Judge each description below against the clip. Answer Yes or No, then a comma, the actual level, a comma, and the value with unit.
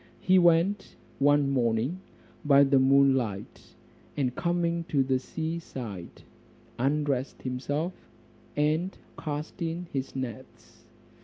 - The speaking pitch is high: No, medium, 145 Hz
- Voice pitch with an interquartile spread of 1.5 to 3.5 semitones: No, average, 4.1 semitones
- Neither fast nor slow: No, slow, 100 wpm